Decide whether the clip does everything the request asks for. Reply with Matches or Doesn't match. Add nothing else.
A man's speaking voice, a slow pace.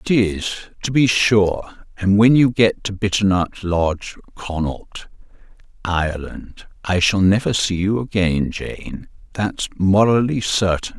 Matches